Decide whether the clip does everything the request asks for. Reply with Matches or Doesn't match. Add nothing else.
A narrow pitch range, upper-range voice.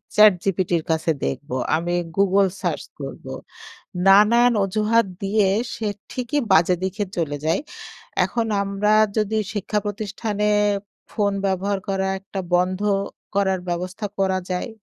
Matches